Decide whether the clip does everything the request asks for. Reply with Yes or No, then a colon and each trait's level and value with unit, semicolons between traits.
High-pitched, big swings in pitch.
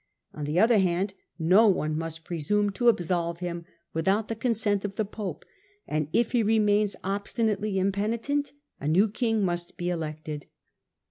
No: high, 195 Hz; average, 4.1 semitones